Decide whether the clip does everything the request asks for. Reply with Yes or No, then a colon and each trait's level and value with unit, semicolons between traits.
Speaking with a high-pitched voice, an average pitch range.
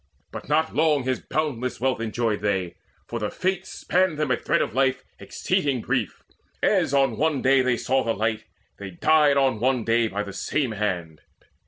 No: low, 130 Hz; average, 4.6 semitones